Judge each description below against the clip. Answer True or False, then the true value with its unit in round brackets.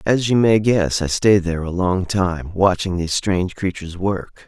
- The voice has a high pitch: False (95 Hz)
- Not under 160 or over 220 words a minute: True (200 wpm)